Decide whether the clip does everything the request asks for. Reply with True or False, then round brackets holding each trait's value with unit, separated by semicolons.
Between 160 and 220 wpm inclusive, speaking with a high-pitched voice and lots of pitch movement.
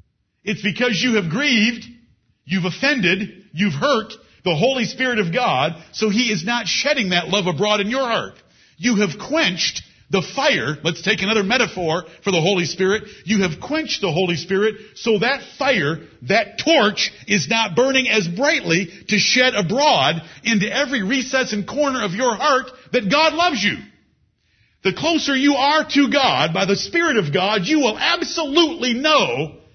True (170 wpm; 215 Hz; 5.7 semitones)